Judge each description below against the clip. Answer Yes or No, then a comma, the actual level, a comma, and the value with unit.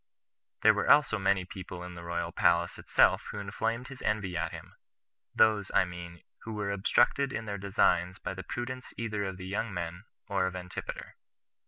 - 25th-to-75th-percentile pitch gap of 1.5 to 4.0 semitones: Yes, average, 3.3 semitones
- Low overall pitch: Yes, very low, 95 Hz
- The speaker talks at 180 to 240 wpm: Yes, average, 185 wpm